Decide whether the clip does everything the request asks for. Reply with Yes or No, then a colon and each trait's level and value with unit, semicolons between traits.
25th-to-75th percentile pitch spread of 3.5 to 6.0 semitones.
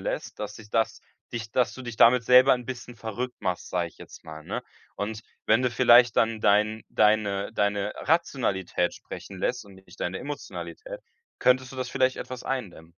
Yes: average, 3.8 semitones